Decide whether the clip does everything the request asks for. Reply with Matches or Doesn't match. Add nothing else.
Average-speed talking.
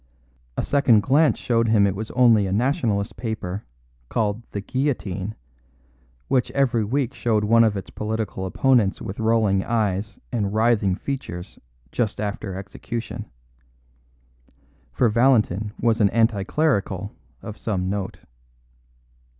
Doesn't match